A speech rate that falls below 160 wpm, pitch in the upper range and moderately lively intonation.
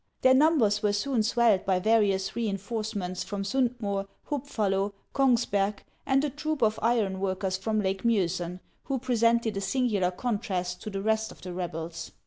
No: average, 165 wpm; high, 210 Hz; average, 3.7 semitones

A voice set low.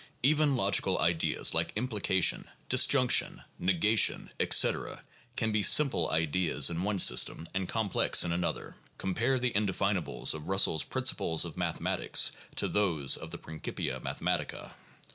Yes: very low, 95 Hz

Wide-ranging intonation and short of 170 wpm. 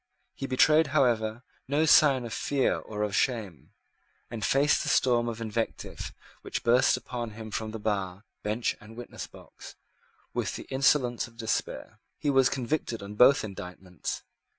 No: average, 3.5 semitones; average, 150 wpm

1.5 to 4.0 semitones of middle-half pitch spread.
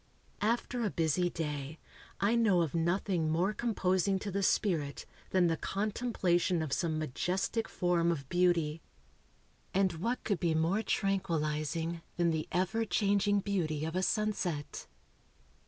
Yes: average, 3.7 semitones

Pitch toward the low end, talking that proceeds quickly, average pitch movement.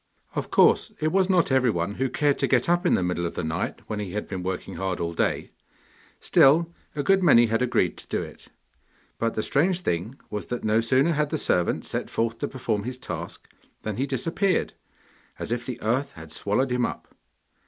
No: low, 125 Hz; fast, 210 wpm; wide, 5.8 semitones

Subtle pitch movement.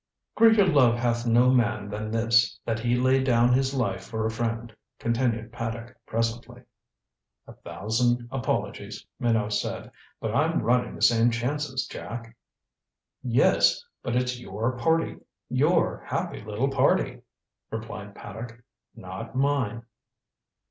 Yes: narrow, 1.9 semitones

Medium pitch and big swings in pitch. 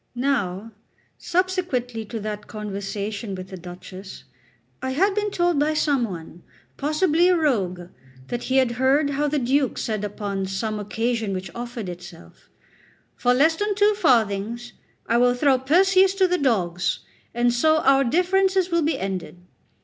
No: high, 245 Hz; wide, 7.3 semitones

